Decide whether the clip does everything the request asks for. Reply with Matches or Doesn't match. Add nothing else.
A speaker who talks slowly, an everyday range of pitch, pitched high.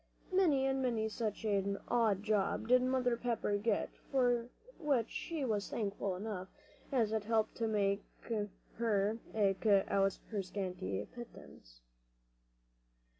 Matches